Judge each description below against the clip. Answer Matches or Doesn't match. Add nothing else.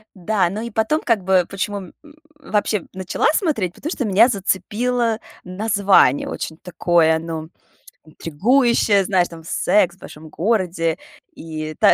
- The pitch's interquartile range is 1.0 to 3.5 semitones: Doesn't match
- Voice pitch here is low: Doesn't match